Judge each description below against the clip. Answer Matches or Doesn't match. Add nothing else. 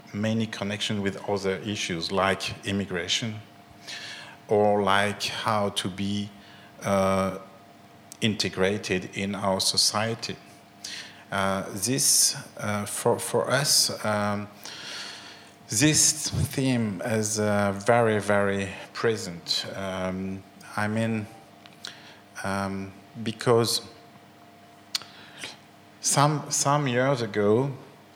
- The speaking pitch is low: Matches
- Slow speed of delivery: Matches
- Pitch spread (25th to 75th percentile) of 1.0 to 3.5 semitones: Matches